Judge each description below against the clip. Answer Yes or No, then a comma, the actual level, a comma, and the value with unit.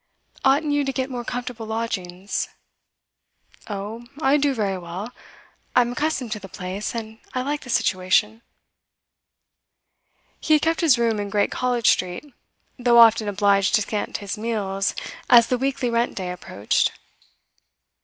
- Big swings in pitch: No, average, 3.9 semitones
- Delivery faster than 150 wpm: No, average, 145 wpm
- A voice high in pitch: Yes, high, 230 Hz